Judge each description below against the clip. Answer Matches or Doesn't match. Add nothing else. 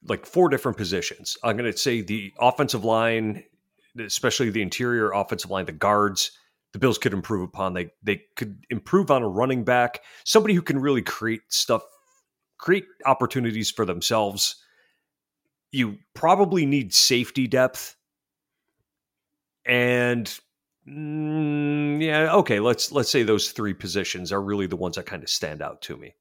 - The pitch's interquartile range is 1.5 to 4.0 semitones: Doesn't match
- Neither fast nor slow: Matches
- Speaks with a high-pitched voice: Doesn't match